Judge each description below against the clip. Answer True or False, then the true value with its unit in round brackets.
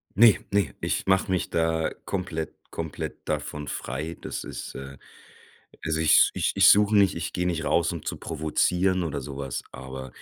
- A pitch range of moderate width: True (3.8 semitones)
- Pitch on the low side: True (80 Hz)